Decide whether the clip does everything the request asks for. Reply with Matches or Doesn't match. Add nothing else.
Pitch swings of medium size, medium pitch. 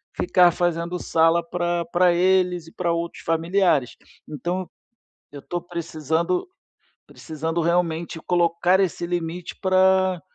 Doesn't match